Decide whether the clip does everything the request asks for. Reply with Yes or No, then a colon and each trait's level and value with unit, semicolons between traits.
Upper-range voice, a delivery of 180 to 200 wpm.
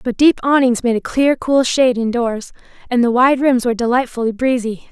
Yes: high, 245 Hz; average, 195 wpm